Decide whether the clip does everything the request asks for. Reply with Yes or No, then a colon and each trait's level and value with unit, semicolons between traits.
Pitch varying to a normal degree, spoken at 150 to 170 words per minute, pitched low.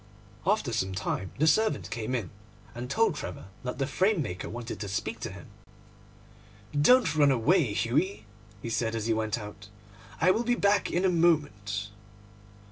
No: wide, 8.5 semitones; average, 165 wpm; low, 125 Hz